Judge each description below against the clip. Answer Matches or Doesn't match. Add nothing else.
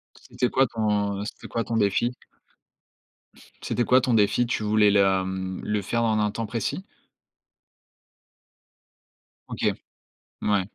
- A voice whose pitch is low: Matches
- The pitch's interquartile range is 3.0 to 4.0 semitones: Doesn't match